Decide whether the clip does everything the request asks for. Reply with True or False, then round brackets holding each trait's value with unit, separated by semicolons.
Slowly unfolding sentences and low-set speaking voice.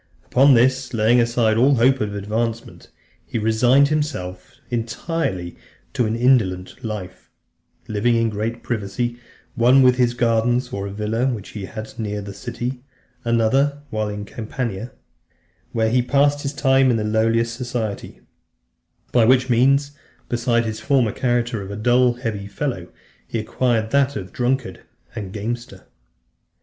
False (150 wpm; 115 Hz)